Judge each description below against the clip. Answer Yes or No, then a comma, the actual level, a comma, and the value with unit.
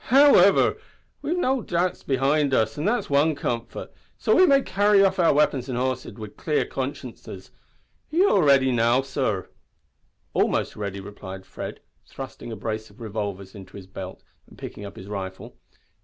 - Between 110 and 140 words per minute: No, average, 170 wpm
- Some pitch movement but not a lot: No, wide, 9.0 semitones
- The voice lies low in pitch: Yes, low, 130 Hz